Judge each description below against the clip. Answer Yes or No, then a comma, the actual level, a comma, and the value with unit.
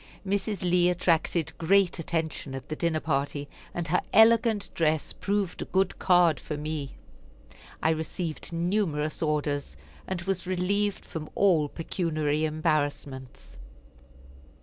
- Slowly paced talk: Yes, slow, 125 wpm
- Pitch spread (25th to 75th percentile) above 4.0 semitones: No, average, 3.4 semitones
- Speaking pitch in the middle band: Yes, medium, 165 Hz